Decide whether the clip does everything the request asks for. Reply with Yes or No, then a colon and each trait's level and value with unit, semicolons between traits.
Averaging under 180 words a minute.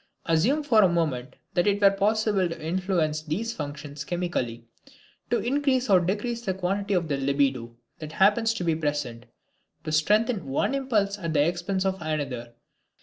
Yes: average, 170 wpm